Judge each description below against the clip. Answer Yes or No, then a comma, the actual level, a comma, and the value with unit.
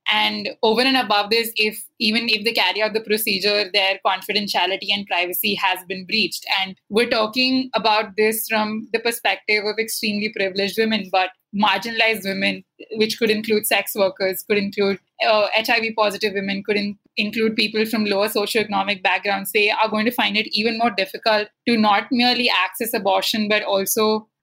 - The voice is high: Yes, high, 215 Hz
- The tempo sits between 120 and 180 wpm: Yes, average, 170 wpm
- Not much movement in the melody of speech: Yes, narrow, 1.9 semitones